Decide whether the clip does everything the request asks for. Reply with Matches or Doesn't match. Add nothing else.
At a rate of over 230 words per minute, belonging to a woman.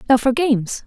Doesn't match